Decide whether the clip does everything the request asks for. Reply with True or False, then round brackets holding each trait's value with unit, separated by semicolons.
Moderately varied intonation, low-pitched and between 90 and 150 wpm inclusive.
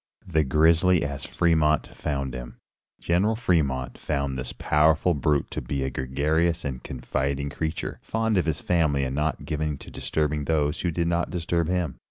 False (3.4 semitones; 75 Hz; 175 wpm)